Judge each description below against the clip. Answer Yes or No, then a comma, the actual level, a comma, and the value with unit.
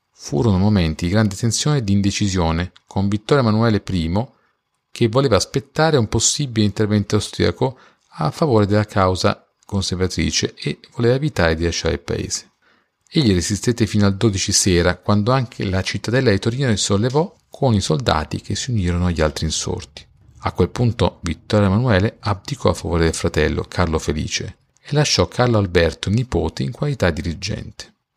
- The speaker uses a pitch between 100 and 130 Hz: Yes, low, 105 Hz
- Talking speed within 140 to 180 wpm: Yes, average, 160 wpm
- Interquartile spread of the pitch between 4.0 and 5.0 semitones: Yes, average, 4.4 semitones